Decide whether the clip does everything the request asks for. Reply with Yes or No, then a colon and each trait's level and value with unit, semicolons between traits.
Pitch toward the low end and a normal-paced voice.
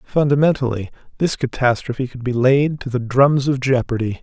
Yes: low, 130 Hz; average, 155 wpm